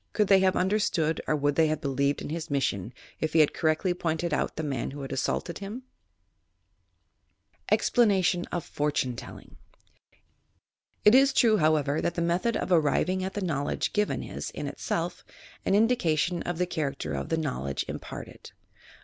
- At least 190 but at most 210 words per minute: No, average, 175 wpm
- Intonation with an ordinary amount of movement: Yes, average, 4.4 semitones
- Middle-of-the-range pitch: Yes, medium, 165 Hz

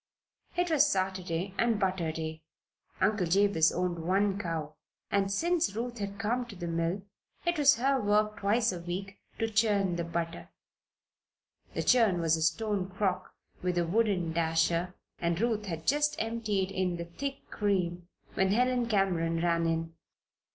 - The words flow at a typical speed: Yes, average, 160 wpm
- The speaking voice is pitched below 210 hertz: Yes, high, 190 Hz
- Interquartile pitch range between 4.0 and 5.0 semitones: Yes, average, 4.4 semitones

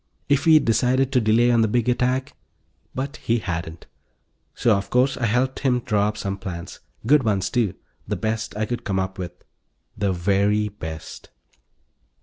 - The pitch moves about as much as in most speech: Yes, average, 4.1 semitones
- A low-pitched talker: Yes, low, 110 Hz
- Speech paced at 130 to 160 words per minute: No, average, 170 wpm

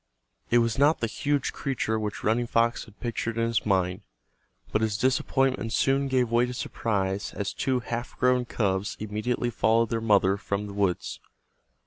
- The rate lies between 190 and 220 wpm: No, average, 170 wpm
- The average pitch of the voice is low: Yes, low, 115 Hz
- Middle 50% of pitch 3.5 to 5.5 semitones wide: No, average, 3.0 semitones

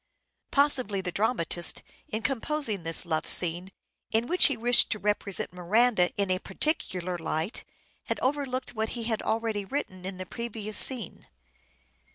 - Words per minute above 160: No, average, 150 wpm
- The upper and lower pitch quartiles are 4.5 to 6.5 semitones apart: Yes, average, 5.0 semitones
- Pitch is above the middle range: Yes, high, 215 Hz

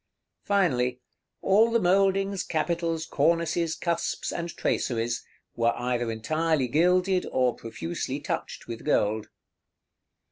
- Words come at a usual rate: No, slow, 105 wpm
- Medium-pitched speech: Yes, medium, 160 Hz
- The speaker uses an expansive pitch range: Yes, wide, 6.8 semitones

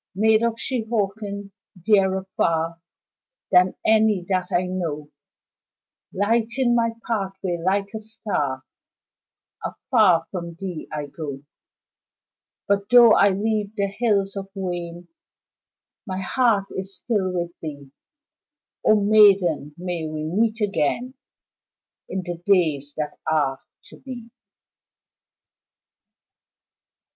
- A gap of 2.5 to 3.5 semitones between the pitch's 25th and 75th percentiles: No, average, 4.1 semitones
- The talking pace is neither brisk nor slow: No, slow, 105 wpm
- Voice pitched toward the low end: No, high, 195 Hz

